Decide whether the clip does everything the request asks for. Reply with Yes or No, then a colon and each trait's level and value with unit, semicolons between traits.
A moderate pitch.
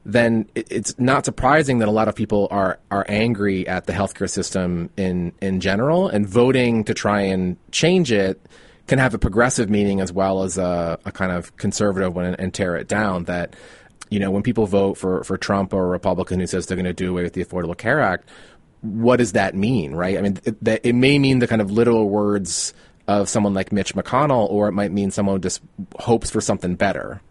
No: low, 100 Hz